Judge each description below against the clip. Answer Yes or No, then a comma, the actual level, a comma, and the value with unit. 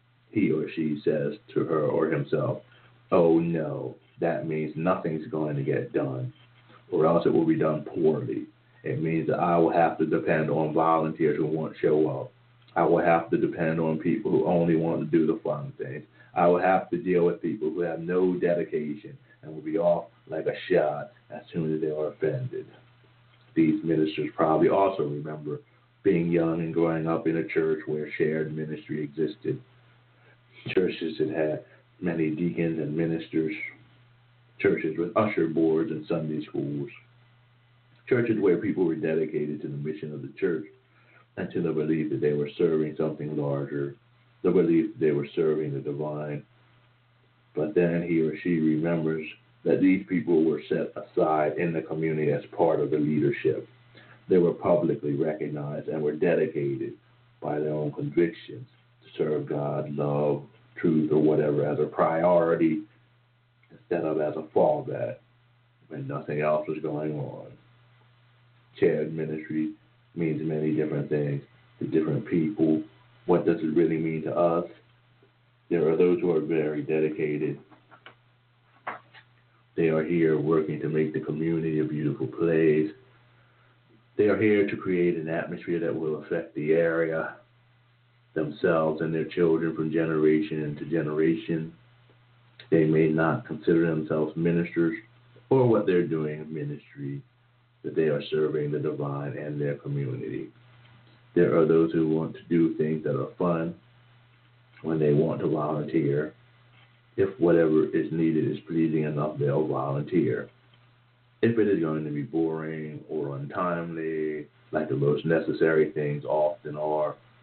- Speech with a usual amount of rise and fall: No, wide, 7.7 semitones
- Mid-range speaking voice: No, very low, 80 Hz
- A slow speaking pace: No, average, 155 wpm